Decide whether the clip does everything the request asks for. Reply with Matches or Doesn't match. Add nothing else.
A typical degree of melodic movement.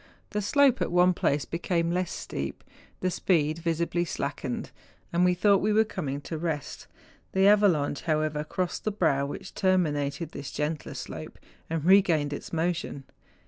Matches